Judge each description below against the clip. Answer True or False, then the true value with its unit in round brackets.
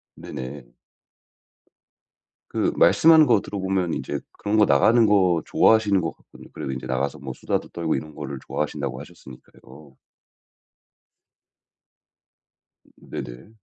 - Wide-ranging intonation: True (7.4 semitones)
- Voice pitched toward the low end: True (80 Hz)